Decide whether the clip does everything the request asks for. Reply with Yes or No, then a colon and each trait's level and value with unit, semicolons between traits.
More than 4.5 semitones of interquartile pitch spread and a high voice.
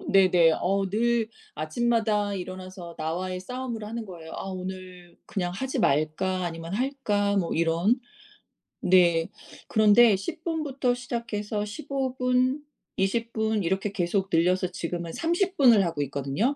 Yes: average, 5.1 semitones; high, 195 Hz